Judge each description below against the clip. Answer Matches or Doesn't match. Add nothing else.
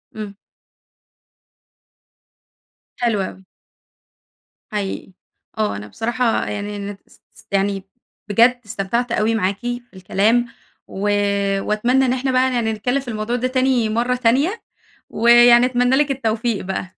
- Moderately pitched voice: Doesn't match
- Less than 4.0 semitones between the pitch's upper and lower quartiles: Matches